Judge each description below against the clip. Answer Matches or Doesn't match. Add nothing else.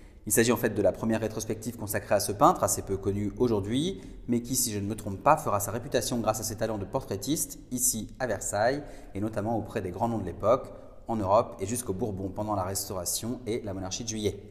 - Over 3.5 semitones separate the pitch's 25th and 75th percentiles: Doesn't match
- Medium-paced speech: Doesn't match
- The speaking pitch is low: Matches